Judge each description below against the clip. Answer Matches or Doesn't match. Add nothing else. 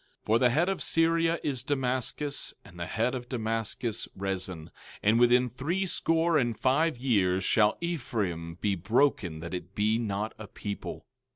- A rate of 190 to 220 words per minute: Doesn't match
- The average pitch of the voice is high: Doesn't match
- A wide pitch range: Matches